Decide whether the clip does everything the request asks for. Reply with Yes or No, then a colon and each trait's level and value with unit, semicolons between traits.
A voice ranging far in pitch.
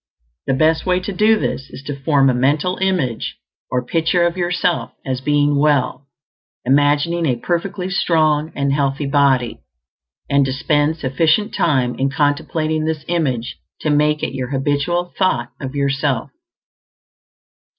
No: average, 3.6 semitones